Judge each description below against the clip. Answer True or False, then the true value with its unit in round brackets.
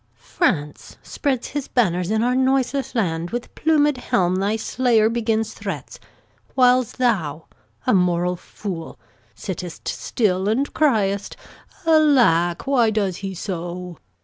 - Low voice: False (220 Hz)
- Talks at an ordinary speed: False (125 wpm)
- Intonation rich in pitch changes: True (6.0 semitones)